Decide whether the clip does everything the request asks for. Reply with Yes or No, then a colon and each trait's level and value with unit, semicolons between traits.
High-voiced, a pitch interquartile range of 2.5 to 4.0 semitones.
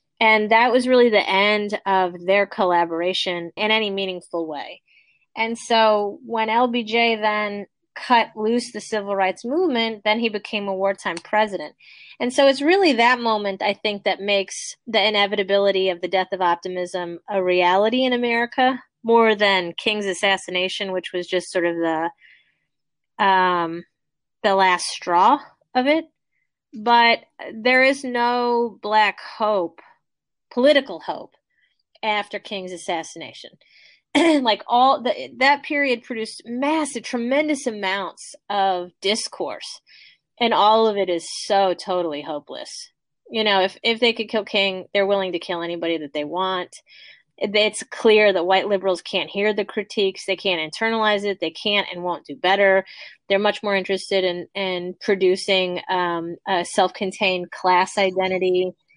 Yes: high, 200 Hz; average, 3.6 semitones